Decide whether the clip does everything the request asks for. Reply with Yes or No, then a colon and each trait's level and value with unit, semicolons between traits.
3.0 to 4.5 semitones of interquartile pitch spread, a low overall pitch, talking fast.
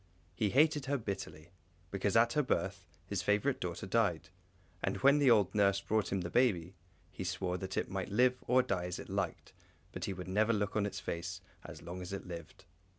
Yes: average, 3.9 semitones; low, 100 Hz; fast, 210 wpm